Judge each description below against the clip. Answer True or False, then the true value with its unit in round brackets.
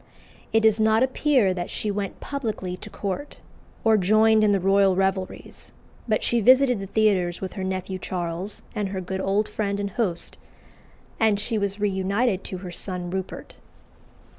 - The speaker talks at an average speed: True (165 wpm)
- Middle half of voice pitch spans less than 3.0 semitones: True (2.5 semitones)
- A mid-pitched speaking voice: False (200 Hz)